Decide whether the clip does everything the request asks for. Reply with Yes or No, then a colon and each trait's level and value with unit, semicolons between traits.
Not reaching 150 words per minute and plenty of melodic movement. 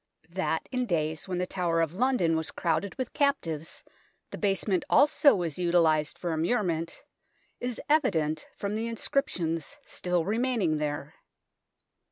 Yes: average, 140 wpm; wide, 5.8 semitones